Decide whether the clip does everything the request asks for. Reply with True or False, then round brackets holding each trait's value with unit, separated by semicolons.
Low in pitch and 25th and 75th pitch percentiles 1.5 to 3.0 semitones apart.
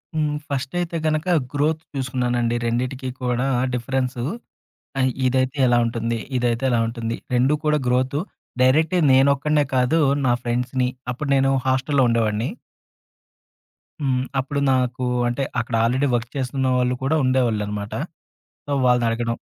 True (130 Hz; 2.4 semitones)